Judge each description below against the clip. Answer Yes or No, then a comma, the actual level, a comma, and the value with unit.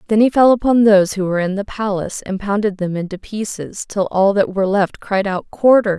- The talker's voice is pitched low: No, high, 200 Hz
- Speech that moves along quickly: Yes, fast, 230 wpm